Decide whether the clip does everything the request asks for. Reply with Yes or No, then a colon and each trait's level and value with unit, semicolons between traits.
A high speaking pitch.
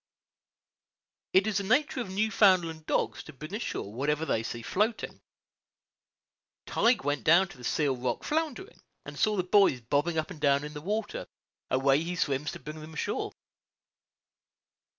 No: medium, 160 Hz